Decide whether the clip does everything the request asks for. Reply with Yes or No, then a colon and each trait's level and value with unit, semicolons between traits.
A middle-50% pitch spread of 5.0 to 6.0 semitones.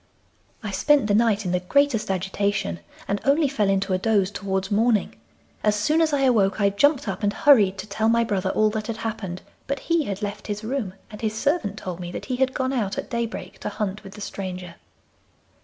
No: average, 3.7 semitones